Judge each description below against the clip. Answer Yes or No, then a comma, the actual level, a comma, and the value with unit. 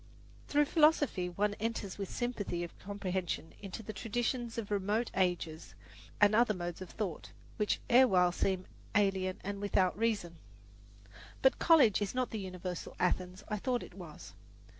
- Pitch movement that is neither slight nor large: Yes, average, 3.8 semitones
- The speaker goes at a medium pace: Yes, average, 150 wpm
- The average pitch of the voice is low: No, high, 200 Hz